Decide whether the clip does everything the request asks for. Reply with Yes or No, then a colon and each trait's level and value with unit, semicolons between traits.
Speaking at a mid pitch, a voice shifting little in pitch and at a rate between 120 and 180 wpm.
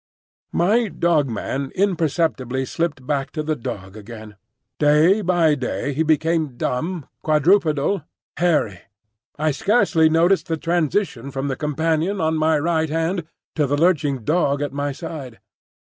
No: medium, 155 Hz; average, 3.5 semitones; average, 140 wpm